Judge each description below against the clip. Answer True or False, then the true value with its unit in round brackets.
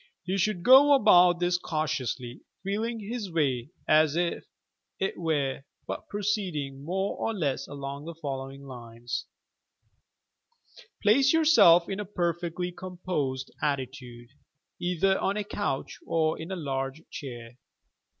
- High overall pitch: False (165 Hz)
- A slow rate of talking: True (120 wpm)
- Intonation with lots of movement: True (5.9 semitones)